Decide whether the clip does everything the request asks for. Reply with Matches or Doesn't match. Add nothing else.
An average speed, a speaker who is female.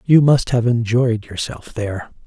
Doesn't match